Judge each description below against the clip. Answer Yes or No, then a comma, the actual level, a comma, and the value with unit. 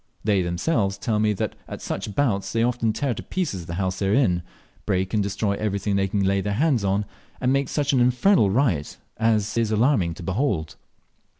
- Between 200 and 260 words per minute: Yes, fast, 205 wpm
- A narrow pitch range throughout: No, average, 4.1 semitones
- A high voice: No, low, 105 Hz